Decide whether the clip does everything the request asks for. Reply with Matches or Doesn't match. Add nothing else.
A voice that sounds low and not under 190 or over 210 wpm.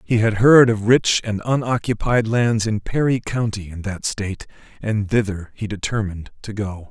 Doesn't match